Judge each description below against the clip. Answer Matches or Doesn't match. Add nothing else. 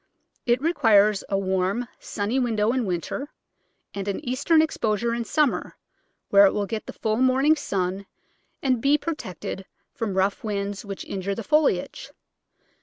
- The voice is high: Matches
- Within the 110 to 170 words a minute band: Matches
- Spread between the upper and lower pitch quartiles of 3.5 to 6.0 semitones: Matches